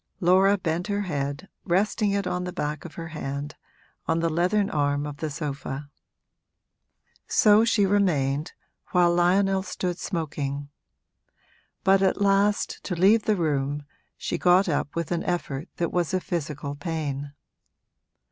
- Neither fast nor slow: Yes, average, 145 wpm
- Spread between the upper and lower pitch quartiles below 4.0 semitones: No, average, 4.8 semitones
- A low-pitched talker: No, medium, 170 Hz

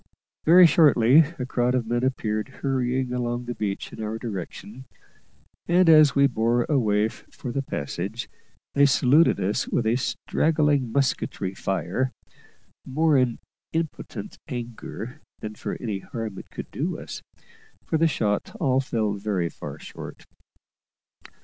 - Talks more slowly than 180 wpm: Yes, average, 140 wpm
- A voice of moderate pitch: No, low, 125 Hz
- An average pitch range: Yes, average, 4.3 semitones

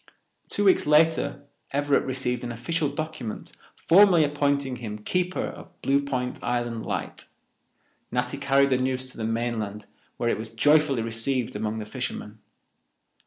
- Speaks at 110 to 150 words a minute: Yes, average, 145 wpm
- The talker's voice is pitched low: Yes, low, 130 Hz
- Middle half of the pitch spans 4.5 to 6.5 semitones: No, average, 3.9 semitones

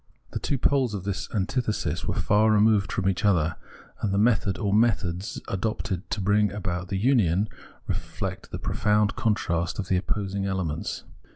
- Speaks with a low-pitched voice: Yes, low, 100 Hz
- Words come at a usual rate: Yes, average, 165 wpm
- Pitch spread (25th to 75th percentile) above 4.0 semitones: No, narrow, 2.4 semitones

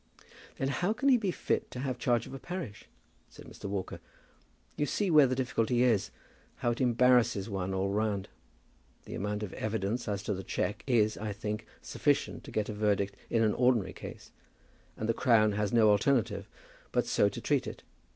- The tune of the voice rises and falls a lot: No, average, 3.4 semitones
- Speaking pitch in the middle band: No, low, 110 Hz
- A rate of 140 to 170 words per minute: No, average, 190 wpm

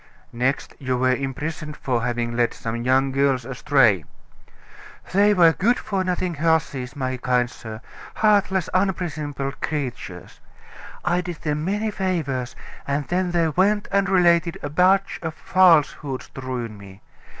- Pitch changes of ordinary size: No, wide, 5.9 semitones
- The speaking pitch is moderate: Yes, medium, 150 Hz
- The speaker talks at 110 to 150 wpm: Yes, average, 140 wpm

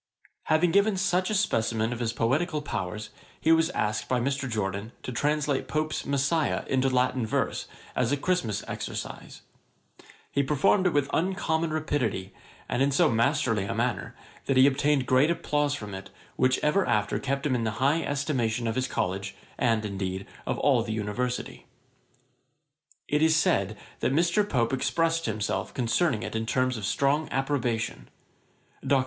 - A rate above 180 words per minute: No, average, 165 wpm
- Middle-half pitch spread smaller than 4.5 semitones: No, average, 5.2 semitones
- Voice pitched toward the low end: Yes, low, 130 Hz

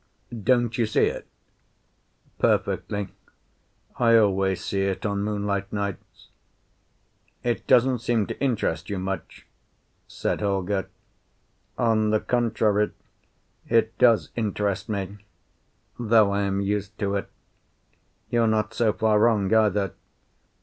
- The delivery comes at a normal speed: No, slow, 115 wpm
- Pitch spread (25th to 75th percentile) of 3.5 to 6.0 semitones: No, narrow, 2.4 semitones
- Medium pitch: No, low, 105 Hz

